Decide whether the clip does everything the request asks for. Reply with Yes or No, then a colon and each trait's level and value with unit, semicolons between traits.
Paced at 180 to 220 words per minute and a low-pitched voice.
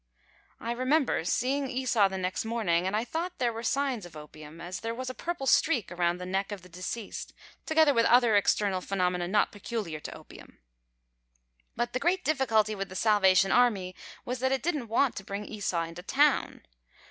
No: average, 185 wpm; high, 220 Hz